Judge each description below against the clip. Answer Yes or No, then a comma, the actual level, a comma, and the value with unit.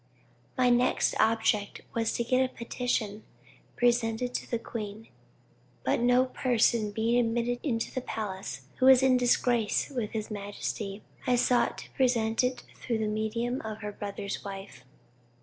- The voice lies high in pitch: Yes, high, 230 Hz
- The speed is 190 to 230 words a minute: No, average, 150 wpm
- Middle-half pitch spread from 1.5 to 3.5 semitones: Yes, narrow, 2.5 semitones